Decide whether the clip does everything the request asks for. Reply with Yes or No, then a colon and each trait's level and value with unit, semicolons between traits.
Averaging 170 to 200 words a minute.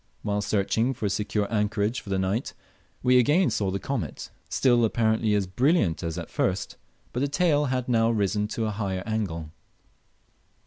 Yes: average, 175 wpm